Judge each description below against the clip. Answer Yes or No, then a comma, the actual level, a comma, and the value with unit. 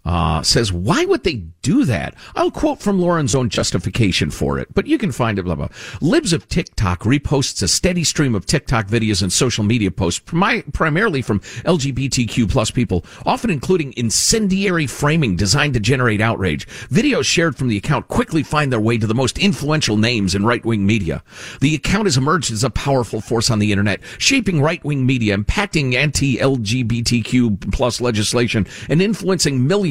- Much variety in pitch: Yes, wide, 6.1 semitones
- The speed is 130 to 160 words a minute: No, average, 185 wpm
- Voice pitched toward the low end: Yes, low, 125 Hz